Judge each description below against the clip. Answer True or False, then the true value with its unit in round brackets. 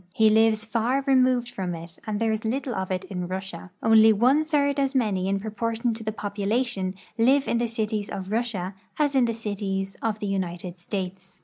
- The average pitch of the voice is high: True (220 Hz)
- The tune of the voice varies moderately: True (3.7 semitones)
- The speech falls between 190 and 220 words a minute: True (195 wpm)